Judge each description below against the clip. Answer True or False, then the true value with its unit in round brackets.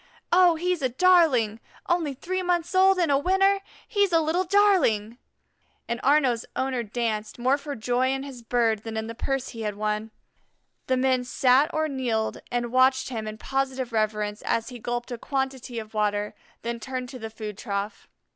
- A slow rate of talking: False (185 wpm)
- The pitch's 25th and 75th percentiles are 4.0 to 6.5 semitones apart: True (4.9 semitones)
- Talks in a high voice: True (255 Hz)